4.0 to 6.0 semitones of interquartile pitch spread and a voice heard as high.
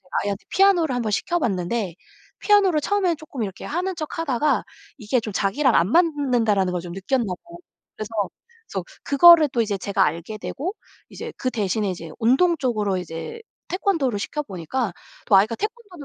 No: wide, 8.6 semitones; high, 245 Hz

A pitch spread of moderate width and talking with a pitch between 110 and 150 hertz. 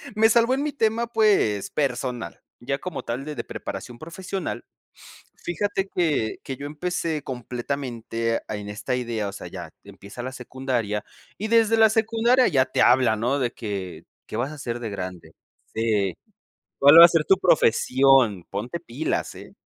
No: wide, 7.6 semitones; low, 135 Hz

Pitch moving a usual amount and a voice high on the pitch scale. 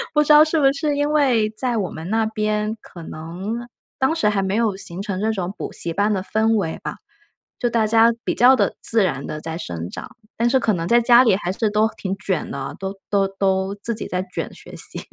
Yes: average, 3.7 semitones; high, 210 Hz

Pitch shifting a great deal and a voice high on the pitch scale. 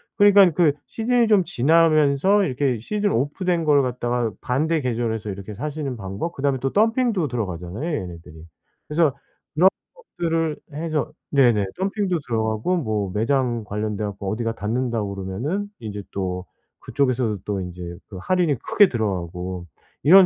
No: wide, 7.9 semitones; low, 130 Hz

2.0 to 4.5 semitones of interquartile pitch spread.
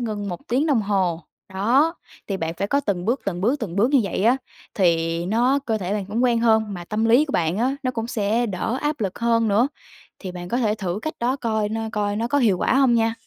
Yes: average, 3.9 semitones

